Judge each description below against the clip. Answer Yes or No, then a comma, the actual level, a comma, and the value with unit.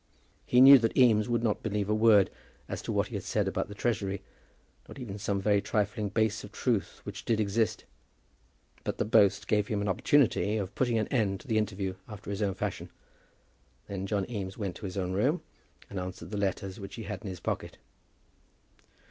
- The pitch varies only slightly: Yes, narrow, 2.2 semitones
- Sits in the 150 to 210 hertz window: No, low, 105 Hz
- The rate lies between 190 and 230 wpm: Yes, average, 200 wpm